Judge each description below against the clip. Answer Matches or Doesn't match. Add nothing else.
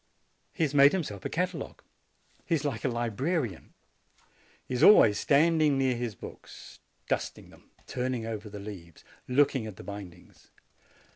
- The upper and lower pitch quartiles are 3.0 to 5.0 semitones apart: Doesn't match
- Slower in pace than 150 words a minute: Doesn't match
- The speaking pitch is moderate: Doesn't match